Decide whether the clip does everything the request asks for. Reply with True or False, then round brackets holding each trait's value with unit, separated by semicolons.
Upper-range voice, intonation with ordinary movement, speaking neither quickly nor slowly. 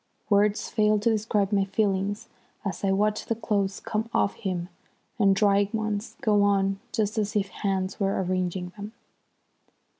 False (200 Hz; 1.5 semitones; 155 wpm)